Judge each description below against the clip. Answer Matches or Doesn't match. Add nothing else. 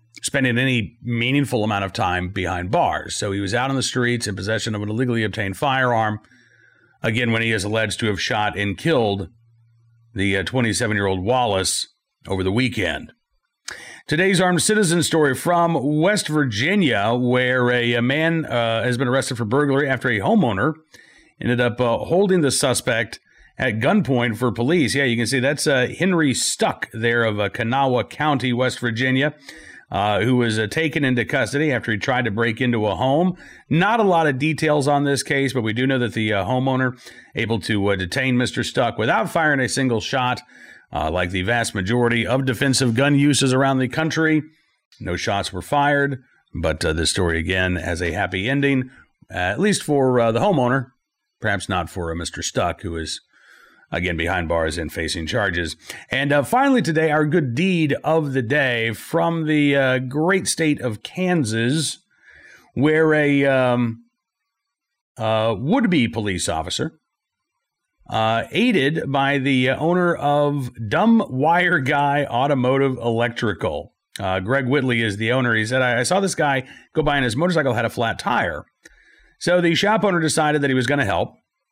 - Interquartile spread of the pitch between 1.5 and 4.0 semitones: Doesn't match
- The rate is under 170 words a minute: Doesn't match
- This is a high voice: Doesn't match